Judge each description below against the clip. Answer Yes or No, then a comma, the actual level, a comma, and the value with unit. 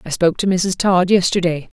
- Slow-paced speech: No, average, 200 wpm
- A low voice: No, medium, 180 Hz